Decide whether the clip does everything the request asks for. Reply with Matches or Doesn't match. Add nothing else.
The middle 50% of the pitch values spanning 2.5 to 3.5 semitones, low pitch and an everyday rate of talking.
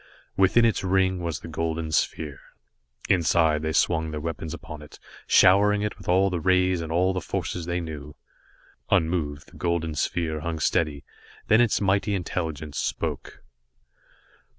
Matches